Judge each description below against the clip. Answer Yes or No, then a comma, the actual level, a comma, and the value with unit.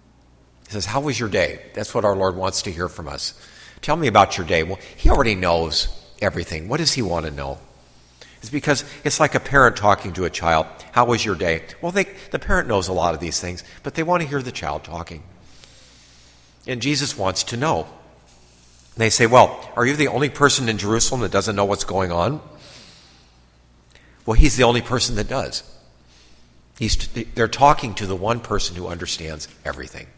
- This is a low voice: Yes, very low, 95 Hz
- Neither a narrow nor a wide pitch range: No, wide, 7.8 semitones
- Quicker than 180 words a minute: Yes, fast, 205 wpm